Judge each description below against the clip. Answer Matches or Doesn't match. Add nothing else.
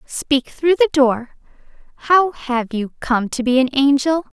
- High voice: Matches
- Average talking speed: Matches